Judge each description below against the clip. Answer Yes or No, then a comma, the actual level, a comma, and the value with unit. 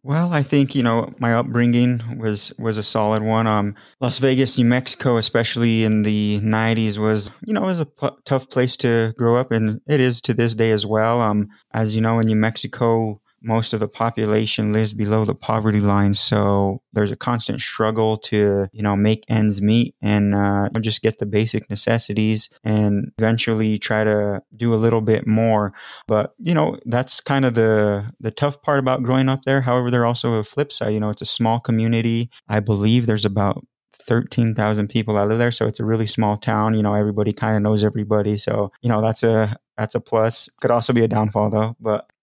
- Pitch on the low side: Yes, low, 110 Hz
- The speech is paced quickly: Yes, fast, 210 wpm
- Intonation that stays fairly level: Yes, narrow, 2.1 semitones